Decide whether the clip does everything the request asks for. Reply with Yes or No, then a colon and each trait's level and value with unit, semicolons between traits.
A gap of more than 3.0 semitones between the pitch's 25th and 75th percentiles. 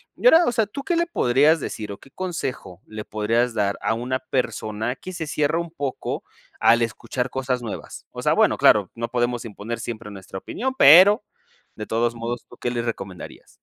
Yes: average, 5.3 semitones